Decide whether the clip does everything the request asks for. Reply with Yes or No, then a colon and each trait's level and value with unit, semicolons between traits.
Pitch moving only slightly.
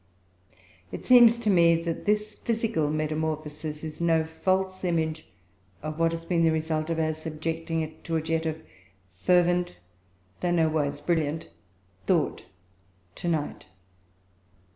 Yes: narrow, 2.0 semitones